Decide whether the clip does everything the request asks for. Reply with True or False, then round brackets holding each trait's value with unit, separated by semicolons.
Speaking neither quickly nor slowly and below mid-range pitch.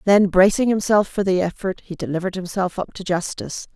False (190 wpm; 190 Hz)